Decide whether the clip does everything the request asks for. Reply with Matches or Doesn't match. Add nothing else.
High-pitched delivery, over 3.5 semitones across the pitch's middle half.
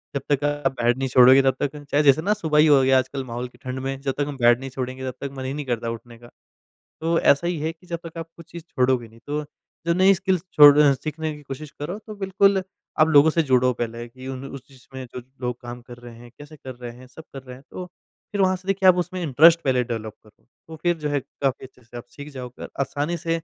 Doesn't match